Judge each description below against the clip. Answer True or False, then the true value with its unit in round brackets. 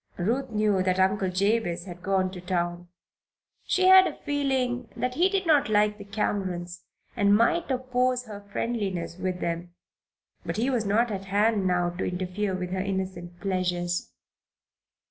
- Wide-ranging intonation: False (4.5 semitones)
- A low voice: False (200 Hz)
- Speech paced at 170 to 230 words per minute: False (160 wpm)